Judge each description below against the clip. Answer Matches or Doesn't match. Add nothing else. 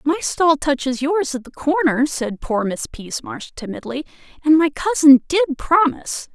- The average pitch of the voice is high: Matches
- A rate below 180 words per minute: Matches